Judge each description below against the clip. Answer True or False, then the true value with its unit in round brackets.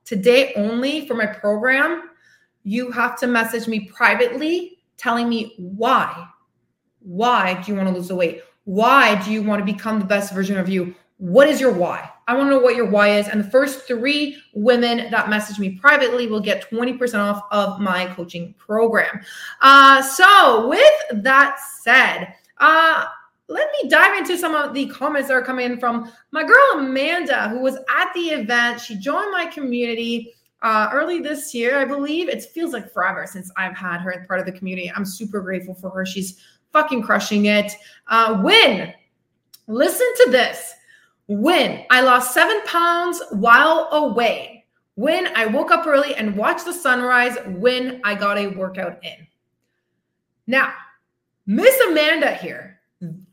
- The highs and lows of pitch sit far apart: True (5.7 semitones)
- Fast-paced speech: False (170 wpm)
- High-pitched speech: True (240 Hz)